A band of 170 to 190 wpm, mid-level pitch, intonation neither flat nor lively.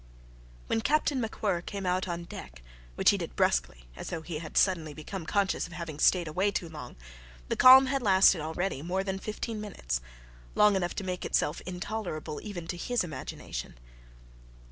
Yes: average, 175 wpm; medium, 180 Hz; average, 4.3 semitones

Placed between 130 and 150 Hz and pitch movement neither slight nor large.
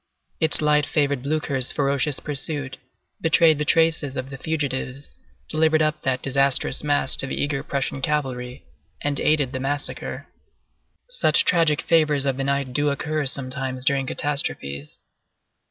No: medium, 140 Hz; narrow, 2.2 semitones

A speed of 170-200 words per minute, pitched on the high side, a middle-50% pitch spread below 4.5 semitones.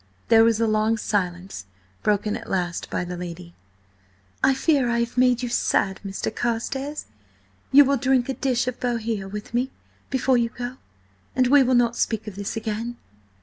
Yes: average, 180 wpm; high, 235 Hz; average, 3.5 semitones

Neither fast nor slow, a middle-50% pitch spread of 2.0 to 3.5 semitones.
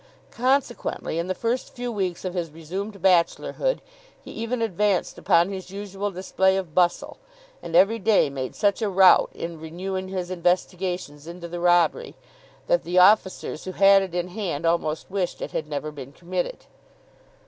Yes: average, 165 wpm; average, 2.8 semitones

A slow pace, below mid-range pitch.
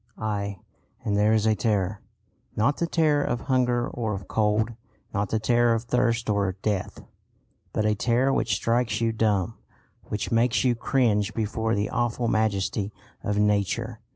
No: average, 160 wpm; low, 110 Hz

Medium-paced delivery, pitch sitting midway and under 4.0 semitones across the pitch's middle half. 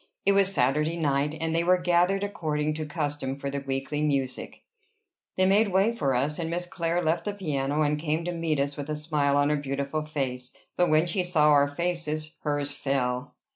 No: fast, 210 wpm; medium, 150 Hz; average, 3.2 semitones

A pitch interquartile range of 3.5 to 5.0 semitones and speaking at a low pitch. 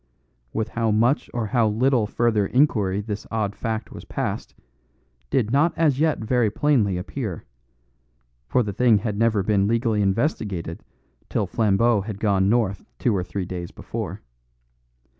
No: average, 3.1 semitones; low, 110 Hz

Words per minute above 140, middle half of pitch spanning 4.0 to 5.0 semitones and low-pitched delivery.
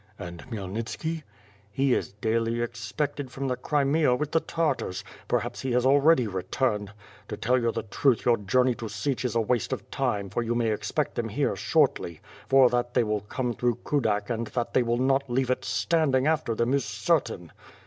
No: average, 185 wpm; average, 3.5 semitones; low, 120 Hz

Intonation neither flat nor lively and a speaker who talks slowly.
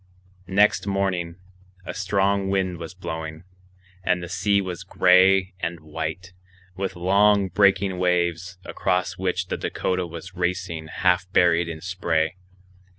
No: narrow, 1.9 semitones; slow, 130 wpm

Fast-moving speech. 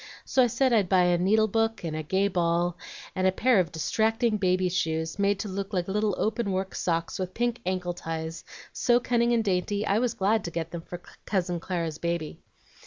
Yes: fast, 210 wpm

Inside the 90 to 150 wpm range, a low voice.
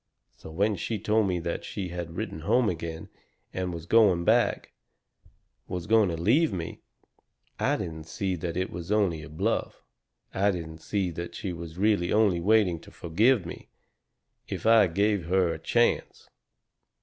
No: average, 165 wpm; very low, 90 Hz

